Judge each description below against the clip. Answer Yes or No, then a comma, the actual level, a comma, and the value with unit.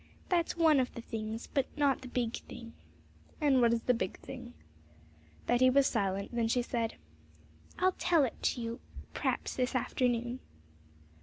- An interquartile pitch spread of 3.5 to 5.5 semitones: No, average, 2.8 semitones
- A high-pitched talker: Yes, high, 245 Hz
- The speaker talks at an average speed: Yes, average, 160 wpm